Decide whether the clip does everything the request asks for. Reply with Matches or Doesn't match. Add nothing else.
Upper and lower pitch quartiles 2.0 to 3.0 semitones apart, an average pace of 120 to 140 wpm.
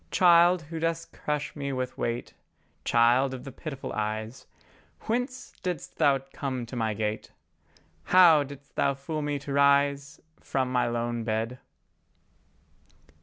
Doesn't match